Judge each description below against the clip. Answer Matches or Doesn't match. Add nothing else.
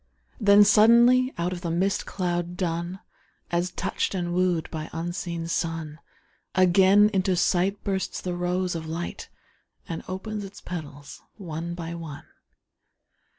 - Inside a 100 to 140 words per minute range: Matches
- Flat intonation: Matches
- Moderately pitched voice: Matches